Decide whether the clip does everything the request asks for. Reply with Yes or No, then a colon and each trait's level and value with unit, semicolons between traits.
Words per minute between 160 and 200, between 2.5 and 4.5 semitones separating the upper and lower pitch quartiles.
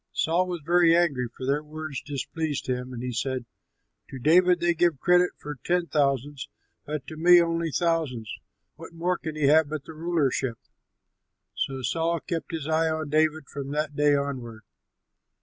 Yes: average, 170 wpm; average, 3.3 semitones